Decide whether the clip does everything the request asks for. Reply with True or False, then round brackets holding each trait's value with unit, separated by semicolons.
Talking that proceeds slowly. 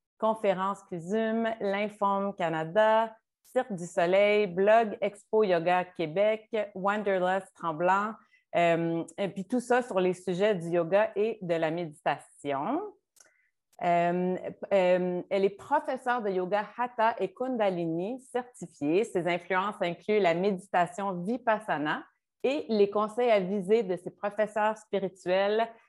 True (125 wpm)